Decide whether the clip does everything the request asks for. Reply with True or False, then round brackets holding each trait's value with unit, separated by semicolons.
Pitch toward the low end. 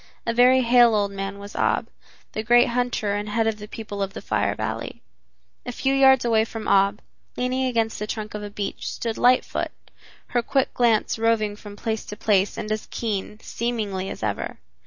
False (220 Hz)